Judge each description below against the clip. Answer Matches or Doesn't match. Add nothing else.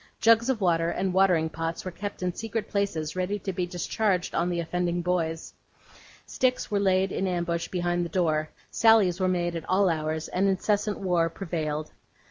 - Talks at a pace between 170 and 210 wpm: Matches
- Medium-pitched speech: Matches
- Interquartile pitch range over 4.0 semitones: Doesn't match